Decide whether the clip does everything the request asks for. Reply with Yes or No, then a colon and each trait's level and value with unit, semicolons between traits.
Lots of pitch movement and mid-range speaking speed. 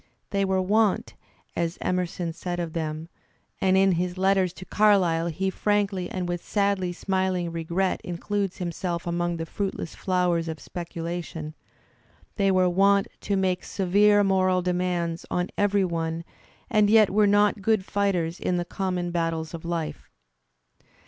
No: narrow, 2.4 semitones; average, 150 wpm